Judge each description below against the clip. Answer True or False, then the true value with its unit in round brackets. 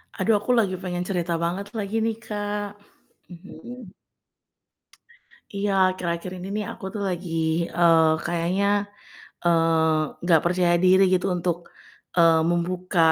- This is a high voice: False (180 Hz)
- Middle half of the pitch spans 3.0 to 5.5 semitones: False (2.6 semitones)